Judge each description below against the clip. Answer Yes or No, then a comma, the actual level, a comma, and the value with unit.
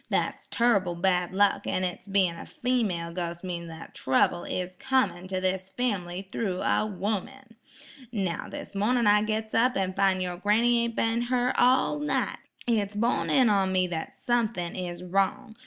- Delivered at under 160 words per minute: No, average, 170 wpm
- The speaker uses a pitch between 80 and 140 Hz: No, high, 195 Hz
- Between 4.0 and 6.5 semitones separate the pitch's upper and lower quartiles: Yes, average, 4.3 semitones